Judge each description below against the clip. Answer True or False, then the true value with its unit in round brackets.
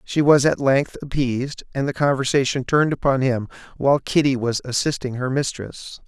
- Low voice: True (130 Hz)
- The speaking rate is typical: True (170 wpm)